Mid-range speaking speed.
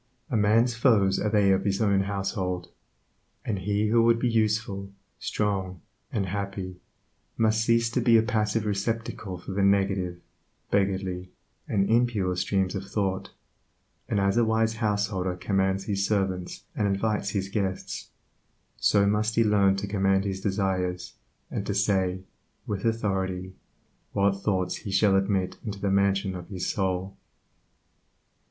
Yes: average, 145 wpm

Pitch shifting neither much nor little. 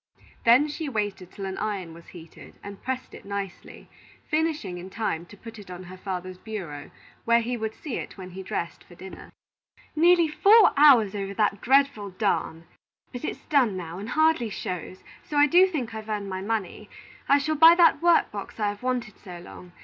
No: wide, 6.9 semitones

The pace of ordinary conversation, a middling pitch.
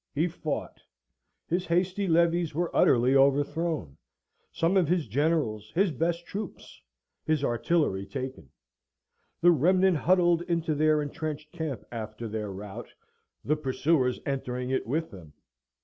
No: slow, 130 wpm; medium, 155 Hz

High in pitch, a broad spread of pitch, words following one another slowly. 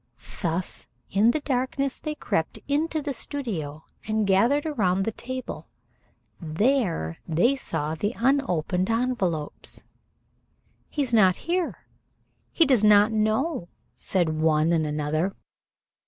Yes: high, 215 Hz; wide, 8.1 semitones; slow, 120 wpm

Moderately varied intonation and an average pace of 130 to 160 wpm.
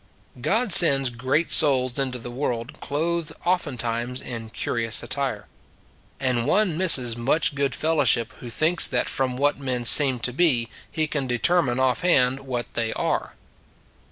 Yes: average, 4.1 semitones; average, 145 wpm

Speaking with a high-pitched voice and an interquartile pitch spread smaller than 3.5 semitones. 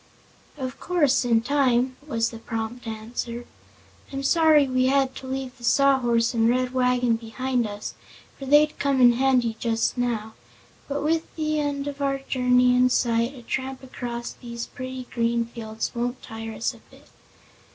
Yes: very high, 250 Hz; narrow, 2.5 semitones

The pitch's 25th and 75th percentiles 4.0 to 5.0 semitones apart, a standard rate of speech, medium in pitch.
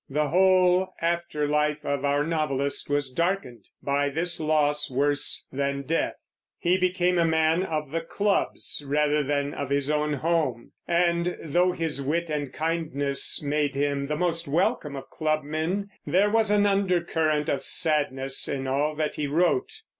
No: average, 3.2 semitones; average, 155 wpm; medium, 155 Hz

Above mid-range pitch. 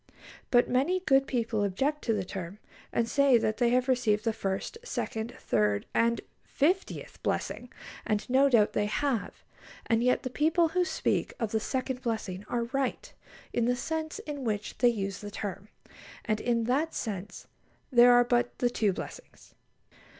Yes: high, 240 Hz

